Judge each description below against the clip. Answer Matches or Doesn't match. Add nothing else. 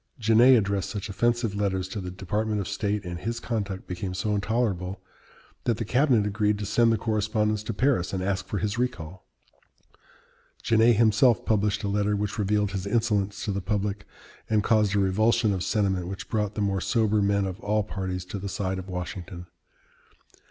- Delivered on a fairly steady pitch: Matches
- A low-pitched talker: Matches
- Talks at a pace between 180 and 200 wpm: Matches